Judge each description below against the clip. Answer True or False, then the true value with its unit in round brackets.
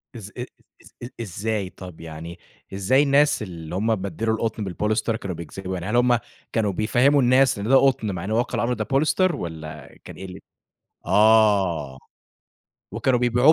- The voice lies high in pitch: False (110 Hz)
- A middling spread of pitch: True (5.0 semitones)